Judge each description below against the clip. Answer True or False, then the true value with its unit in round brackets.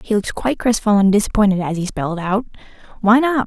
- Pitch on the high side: True (210 Hz)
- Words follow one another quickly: True (210 wpm)